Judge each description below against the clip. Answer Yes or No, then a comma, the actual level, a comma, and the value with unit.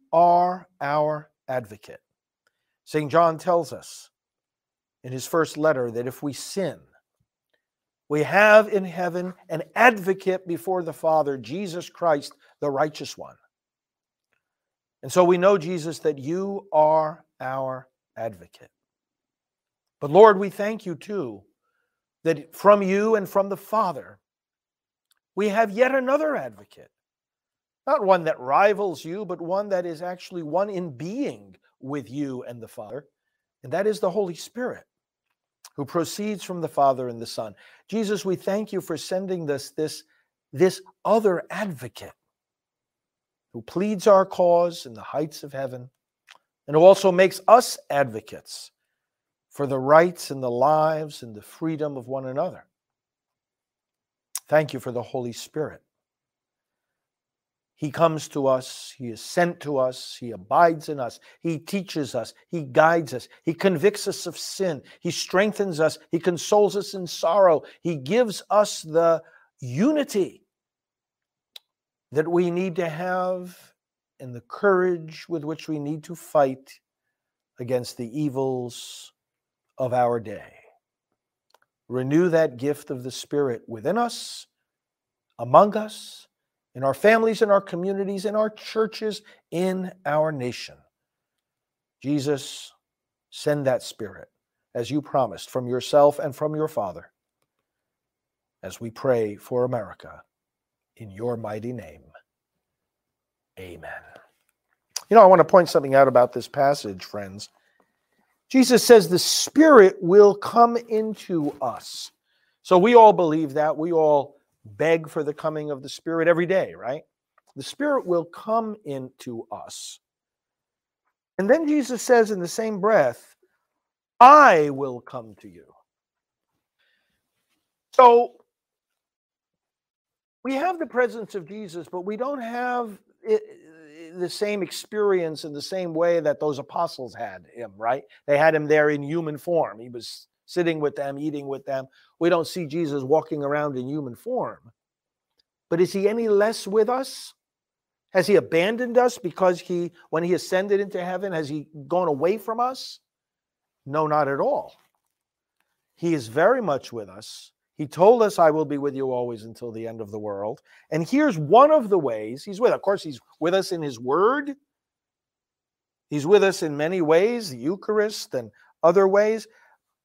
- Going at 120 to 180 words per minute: Yes, average, 145 wpm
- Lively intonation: Yes, wide, 5.9 semitones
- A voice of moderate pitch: Yes, medium, 165 Hz